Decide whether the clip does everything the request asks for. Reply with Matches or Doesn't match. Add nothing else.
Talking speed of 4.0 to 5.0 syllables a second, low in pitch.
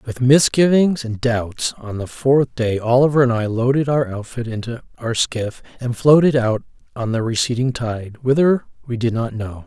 Matches